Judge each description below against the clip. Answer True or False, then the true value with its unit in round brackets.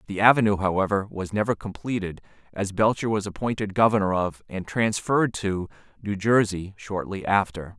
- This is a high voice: False (100 Hz)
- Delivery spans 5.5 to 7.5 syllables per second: False (5.2 syllables/s)